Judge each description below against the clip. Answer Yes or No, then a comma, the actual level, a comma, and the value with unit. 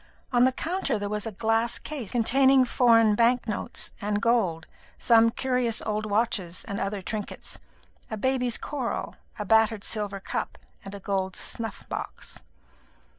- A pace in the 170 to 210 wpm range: No, average, 150 wpm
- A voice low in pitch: No, high, 225 Hz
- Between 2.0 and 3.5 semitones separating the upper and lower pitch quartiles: Yes, average, 2.9 semitones